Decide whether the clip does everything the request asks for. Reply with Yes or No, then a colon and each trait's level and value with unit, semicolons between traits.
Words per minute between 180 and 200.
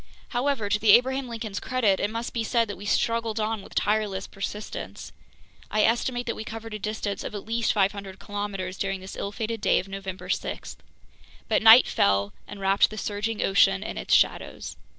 Yes: average, 190 wpm